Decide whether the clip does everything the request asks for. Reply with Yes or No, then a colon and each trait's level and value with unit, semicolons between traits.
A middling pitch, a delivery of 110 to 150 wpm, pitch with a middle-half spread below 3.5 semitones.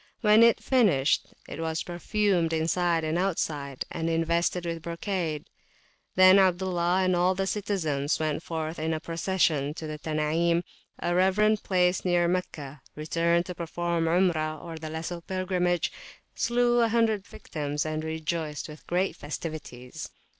Yes: medium, 170 Hz; slow, 135 wpm; average, 2.8 semitones